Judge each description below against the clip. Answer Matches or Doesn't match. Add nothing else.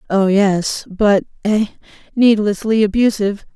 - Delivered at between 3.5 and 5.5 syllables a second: Matches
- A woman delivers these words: Matches